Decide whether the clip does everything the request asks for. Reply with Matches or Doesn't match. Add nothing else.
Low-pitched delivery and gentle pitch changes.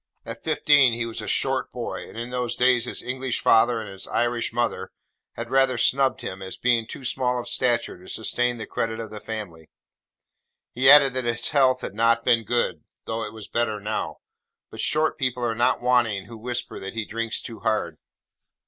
Matches